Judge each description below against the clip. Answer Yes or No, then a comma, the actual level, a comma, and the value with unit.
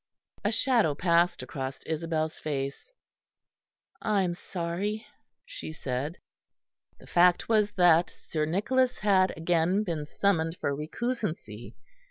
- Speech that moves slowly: Yes, slow, 115 wpm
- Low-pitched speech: No, medium, 175 Hz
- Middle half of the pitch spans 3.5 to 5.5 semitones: Yes, average, 4.7 semitones